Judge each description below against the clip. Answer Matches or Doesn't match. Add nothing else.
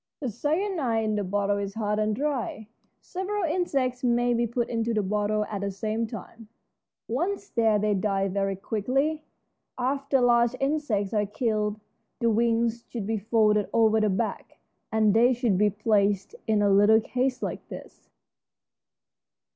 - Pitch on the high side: Matches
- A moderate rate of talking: Matches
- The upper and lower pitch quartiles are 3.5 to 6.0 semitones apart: Doesn't match